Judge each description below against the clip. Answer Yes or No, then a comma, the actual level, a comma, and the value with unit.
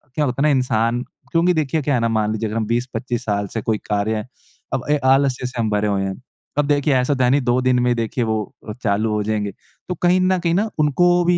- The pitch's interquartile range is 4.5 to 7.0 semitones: Yes, average, 5.0 semitones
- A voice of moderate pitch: No, low, 125 Hz